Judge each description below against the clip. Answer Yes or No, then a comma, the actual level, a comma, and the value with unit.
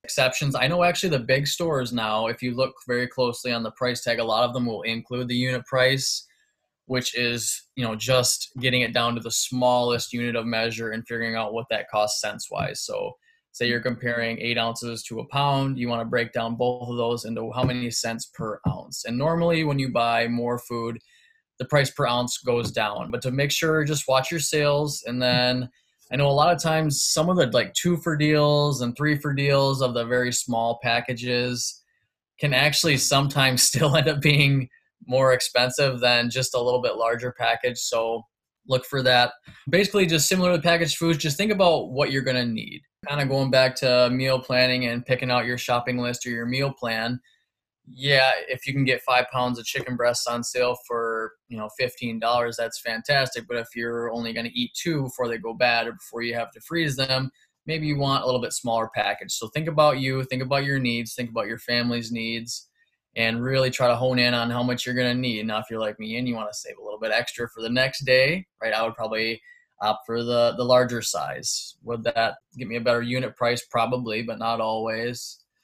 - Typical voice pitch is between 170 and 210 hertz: No, low, 125 Hz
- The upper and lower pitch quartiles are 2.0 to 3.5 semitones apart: Yes, narrow, 2.6 semitones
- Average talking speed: No, fast, 220 wpm